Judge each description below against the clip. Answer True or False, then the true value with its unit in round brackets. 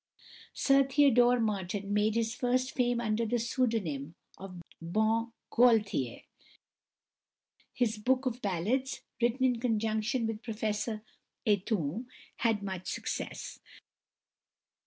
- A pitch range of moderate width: True (3.0 semitones)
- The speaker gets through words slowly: True (105 wpm)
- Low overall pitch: False (225 Hz)